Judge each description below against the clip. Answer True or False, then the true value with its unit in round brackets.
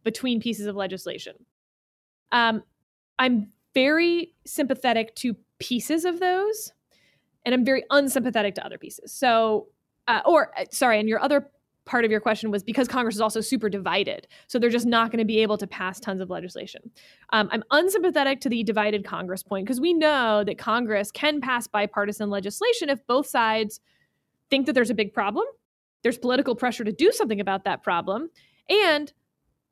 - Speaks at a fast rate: False (175 wpm)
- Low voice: False (235 Hz)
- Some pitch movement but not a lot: True (4.5 semitones)